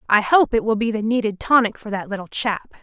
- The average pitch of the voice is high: Yes, high, 220 Hz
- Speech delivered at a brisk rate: Yes, fast, 255 wpm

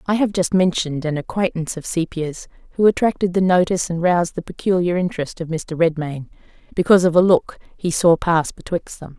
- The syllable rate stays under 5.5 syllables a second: No, 5.9 syllables/s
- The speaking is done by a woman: Yes, female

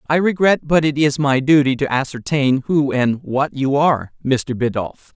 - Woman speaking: No, male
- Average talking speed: Yes, average, 185 wpm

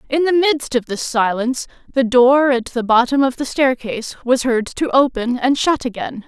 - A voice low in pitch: No, very high, 255 Hz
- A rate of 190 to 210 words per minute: Yes, average, 200 wpm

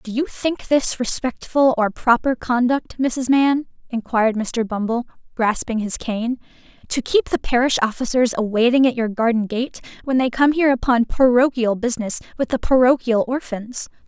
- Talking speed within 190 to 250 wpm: No, average, 160 wpm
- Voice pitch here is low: No, high, 245 Hz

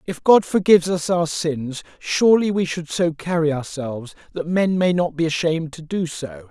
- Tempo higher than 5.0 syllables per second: No, 4.9 syllables/s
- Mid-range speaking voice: Yes, medium, 165 Hz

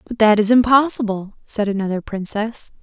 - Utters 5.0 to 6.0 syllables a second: Yes, 5.1 syllables/s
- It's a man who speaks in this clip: No, female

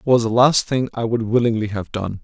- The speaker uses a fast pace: Yes, fast, 270 wpm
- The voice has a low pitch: Yes, low, 115 Hz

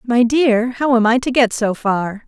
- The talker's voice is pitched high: Yes, high, 235 Hz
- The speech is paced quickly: Yes, fast, 235 wpm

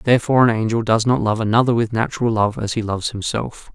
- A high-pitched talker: No, low, 115 Hz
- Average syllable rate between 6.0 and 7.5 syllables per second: Yes, 6.5 syllables/s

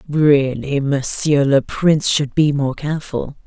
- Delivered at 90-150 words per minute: Yes, average, 140 wpm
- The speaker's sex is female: Yes, female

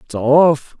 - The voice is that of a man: Yes, male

